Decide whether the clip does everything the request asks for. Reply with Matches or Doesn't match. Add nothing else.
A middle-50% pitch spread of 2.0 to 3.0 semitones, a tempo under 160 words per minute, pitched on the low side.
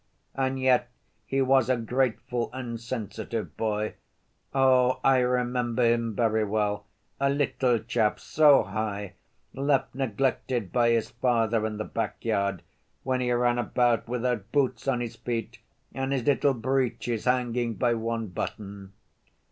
Matches